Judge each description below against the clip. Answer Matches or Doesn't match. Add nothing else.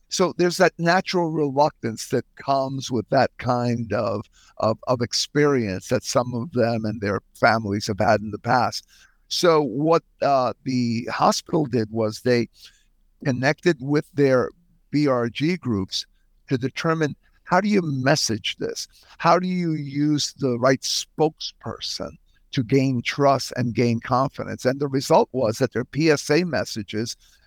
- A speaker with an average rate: Matches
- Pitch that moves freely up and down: Doesn't match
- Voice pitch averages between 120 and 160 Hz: Matches